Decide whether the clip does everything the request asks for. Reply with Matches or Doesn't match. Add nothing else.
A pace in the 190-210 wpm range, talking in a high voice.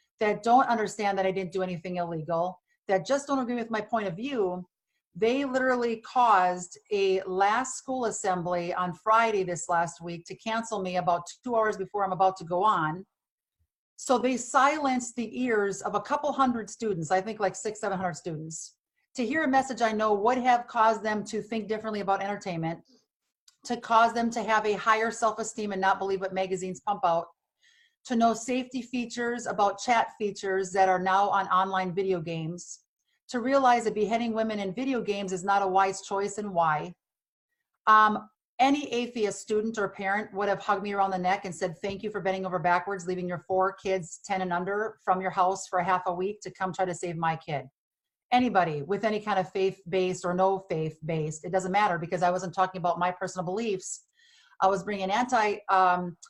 Matches